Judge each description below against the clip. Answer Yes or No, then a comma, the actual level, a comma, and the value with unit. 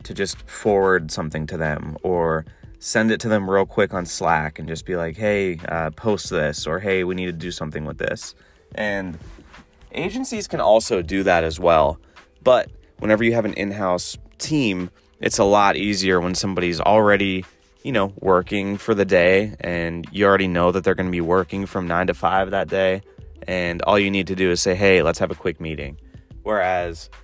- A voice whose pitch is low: Yes, very low, 95 Hz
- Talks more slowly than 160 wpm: No, average, 200 wpm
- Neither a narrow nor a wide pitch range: Yes, average, 3.0 semitones